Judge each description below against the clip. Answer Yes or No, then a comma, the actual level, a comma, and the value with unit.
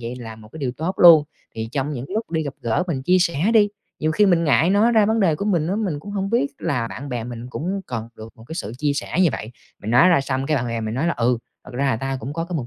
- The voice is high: No, medium, 145 Hz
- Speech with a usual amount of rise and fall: No, wide, 6.7 semitones